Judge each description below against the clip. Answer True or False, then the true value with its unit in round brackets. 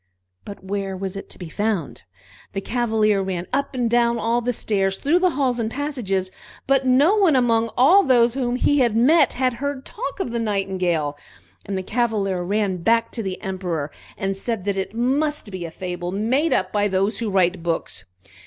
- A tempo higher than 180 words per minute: True (190 wpm)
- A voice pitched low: False (220 Hz)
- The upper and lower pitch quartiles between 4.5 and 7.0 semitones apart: True (4.8 semitones)